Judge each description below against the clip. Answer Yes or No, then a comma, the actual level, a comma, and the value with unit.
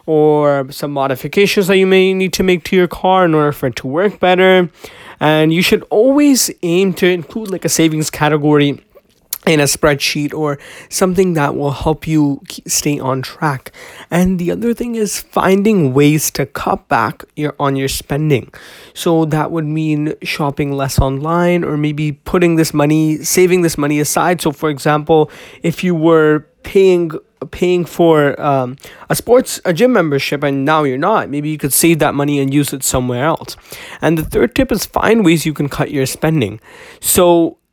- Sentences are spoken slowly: No, average, 185 wpm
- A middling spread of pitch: Yes, average, 3.6 semitones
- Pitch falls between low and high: Yes, medium, 155 Hz